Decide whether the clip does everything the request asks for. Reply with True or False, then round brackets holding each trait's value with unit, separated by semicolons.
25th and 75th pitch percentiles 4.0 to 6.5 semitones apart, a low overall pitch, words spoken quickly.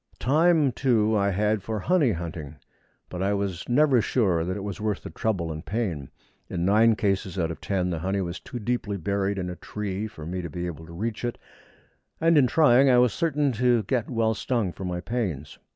True (5.1 semitones; 100 Hz; 215 wpm)